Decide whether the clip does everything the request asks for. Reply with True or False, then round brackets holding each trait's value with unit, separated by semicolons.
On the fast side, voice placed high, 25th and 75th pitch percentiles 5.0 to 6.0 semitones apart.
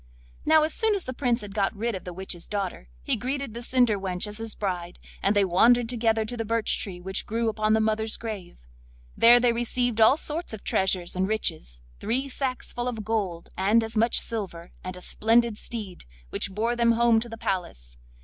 False (210 wpm; 220 Hz; 3.7 semitones)